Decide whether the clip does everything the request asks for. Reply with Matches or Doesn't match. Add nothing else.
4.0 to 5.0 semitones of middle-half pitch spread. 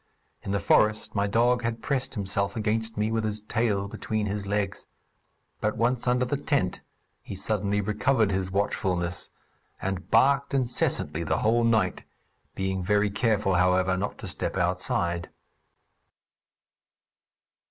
Doesn't match